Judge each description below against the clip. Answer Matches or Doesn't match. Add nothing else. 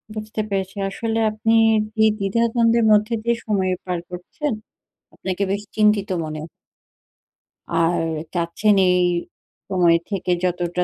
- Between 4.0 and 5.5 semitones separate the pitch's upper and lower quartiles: Doesn't match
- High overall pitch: Matches